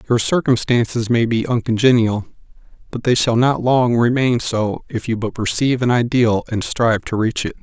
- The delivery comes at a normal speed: Yes, average, 180 wpm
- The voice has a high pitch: No, low, 120 Hz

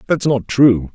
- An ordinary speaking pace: Yes, average, 190 wpm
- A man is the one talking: Yes, male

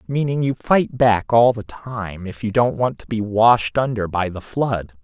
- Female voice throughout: No, male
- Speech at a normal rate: No, fast, 215 wpm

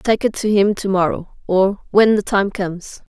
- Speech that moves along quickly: Yes, fast, 210 wpm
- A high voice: Yes, high, 200 Hz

